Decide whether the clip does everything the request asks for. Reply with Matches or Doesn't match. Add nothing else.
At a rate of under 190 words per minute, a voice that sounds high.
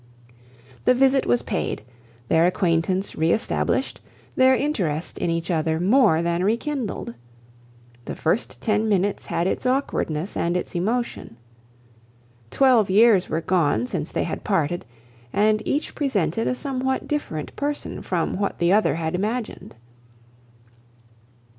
Matches